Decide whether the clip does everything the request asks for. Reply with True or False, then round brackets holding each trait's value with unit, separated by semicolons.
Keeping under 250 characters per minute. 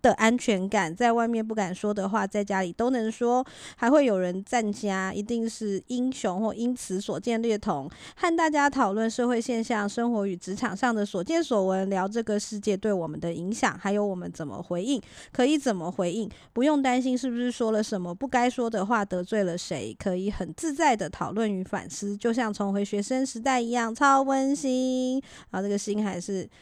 False (300 characters per minute)